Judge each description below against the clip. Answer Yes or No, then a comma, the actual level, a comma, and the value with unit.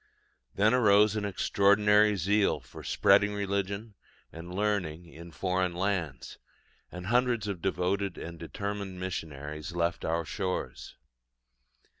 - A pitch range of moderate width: Yes, average, 3.2 semitones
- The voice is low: Yes, very low, 95 Hz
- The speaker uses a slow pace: Yes, slow, 115 wpm